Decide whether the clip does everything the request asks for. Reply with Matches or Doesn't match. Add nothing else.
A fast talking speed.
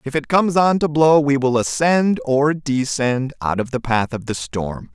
Matches